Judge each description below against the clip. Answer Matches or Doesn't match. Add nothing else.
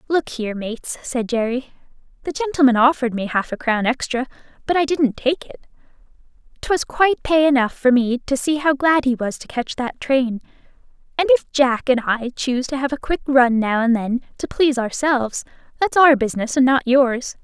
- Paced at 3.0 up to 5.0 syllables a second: Doesn't match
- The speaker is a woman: Matches